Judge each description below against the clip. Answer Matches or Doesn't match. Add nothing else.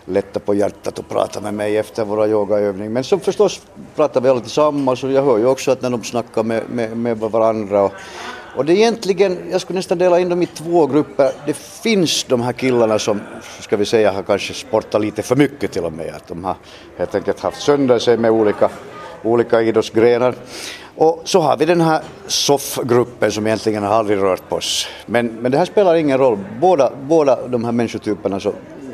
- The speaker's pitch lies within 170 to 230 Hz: Doesn't match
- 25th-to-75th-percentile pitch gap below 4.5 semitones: Doesn't match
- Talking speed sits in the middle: Doesn't match